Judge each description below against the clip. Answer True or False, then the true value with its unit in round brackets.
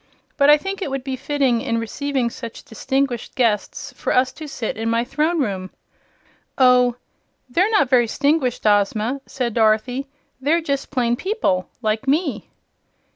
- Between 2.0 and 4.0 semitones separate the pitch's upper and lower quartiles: True (3.7 semitones)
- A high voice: True (255 Hz)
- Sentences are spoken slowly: False (155 wpm)